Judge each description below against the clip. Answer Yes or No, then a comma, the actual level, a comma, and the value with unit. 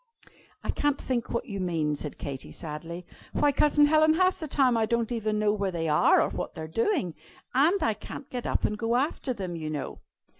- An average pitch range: No, wide, 8.6 semitones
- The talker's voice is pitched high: Yes, high, 220 Hz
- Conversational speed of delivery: No, fast, 220 wpm